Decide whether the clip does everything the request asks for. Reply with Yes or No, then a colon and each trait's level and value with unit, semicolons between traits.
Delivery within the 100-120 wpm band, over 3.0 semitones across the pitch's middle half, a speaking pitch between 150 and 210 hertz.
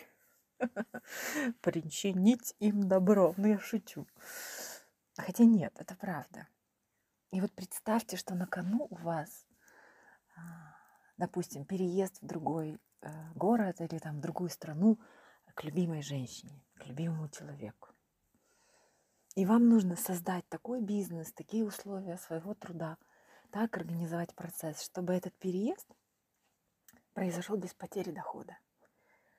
Yes: average, 110 wpm; average, 4.0 semitones; medium, 185 Hz